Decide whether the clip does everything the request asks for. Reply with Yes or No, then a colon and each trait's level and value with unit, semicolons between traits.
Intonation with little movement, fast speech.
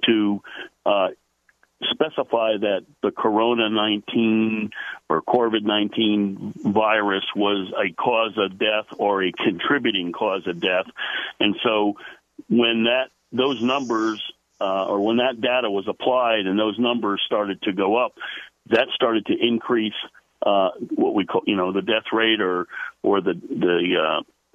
No: narrow, 2.1 semitones; average, 145 wpm